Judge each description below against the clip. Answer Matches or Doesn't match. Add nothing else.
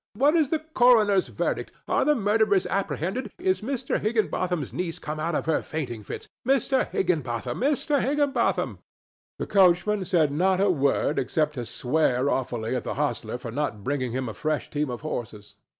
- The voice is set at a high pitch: Doesn't match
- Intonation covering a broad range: Matches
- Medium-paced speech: Matches